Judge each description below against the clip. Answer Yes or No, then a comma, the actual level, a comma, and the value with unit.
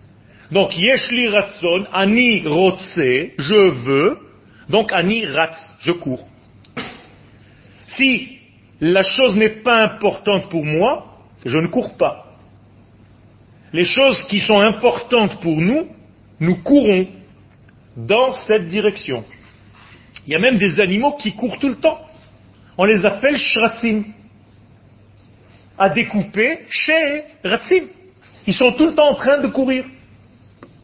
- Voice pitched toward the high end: Yes, high, 195 Hz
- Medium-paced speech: No, slow, 125 wpm